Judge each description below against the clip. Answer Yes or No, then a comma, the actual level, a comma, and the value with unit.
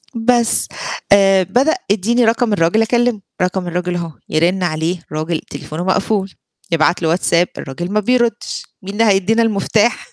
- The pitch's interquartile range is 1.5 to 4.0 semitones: No, average, 4.5 semitones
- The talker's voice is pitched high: Yes, high, 195 Hz